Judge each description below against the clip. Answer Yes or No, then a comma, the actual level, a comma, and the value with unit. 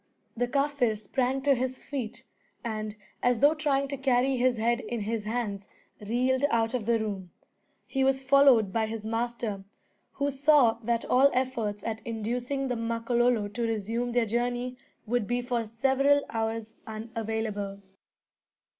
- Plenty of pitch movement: No, average, 2.7 semitones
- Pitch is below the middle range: No, high, 235 Hz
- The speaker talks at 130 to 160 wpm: Yes, average, 150 wpm